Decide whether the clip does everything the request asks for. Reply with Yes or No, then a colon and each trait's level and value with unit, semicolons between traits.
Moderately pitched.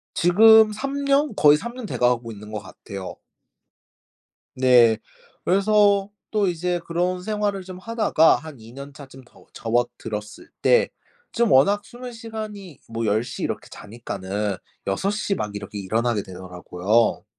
Yes: medium, 160 Hz